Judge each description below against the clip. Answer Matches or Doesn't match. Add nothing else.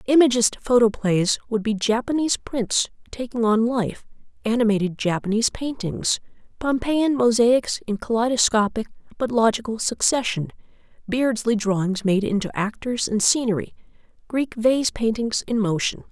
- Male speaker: Doesn't match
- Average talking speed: Doesn't match